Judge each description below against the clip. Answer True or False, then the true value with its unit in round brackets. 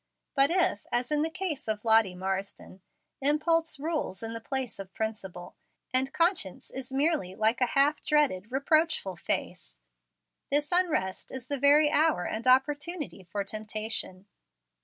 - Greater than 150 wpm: False (145 wpm)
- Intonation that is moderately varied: False (6.8 semitones)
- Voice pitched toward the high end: True (260 Hz)